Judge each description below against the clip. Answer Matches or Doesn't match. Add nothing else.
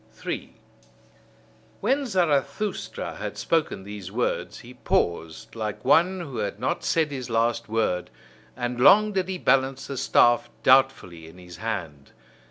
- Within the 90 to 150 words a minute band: Matches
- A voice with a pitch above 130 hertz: Doesn't match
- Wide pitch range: Matches